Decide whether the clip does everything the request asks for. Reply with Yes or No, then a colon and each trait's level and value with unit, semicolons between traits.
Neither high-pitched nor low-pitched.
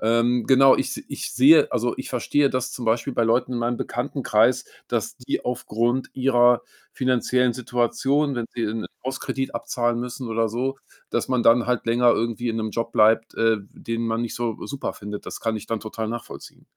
No: low, 120 Hz